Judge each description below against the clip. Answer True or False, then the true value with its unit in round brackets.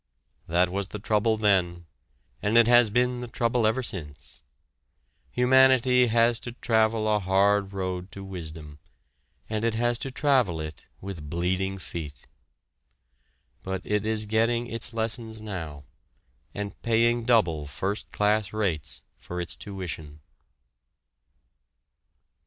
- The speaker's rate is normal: False (125 wpm)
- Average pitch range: True (4.3 semitones)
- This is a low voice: True (105 Hz)